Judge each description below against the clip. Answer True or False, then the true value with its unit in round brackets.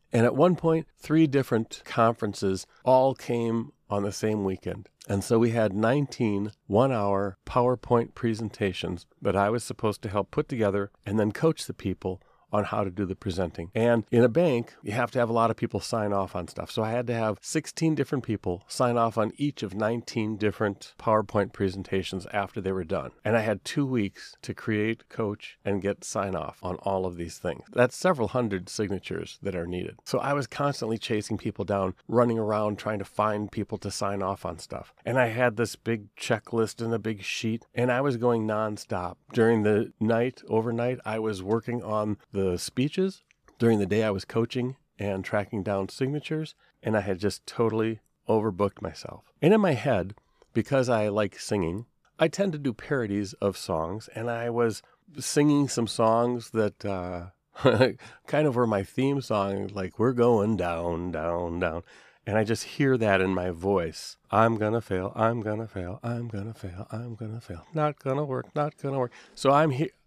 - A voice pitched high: False (110 Hz)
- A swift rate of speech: False (195 wpm)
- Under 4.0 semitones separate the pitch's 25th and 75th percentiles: True (3.5 semitones)